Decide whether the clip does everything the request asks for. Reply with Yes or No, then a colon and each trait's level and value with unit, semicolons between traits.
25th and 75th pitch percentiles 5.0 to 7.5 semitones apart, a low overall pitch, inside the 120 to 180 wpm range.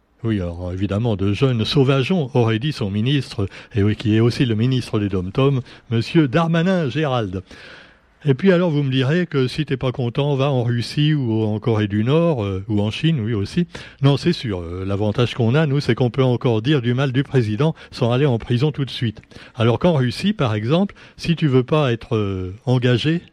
No: average, 5.3 semitones; low, 125 Hz; average, 215 wpm